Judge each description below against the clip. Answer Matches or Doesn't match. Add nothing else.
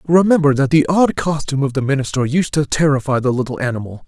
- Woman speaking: Doesn't match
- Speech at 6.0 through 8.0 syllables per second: Matches